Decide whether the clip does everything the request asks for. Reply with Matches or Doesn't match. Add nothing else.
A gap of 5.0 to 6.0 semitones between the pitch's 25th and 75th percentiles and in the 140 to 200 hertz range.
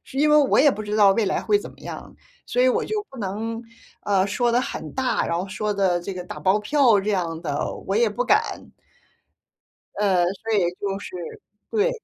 Doesn't match